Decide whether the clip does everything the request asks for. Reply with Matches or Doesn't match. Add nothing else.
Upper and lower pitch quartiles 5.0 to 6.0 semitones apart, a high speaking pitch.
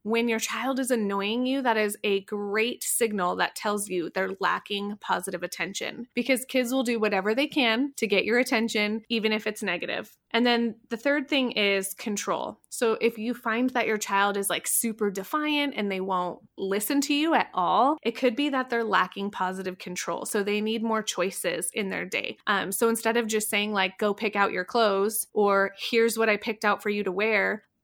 Doesn't match